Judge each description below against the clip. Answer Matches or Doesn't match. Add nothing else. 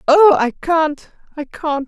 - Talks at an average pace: Matches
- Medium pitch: Doesn't match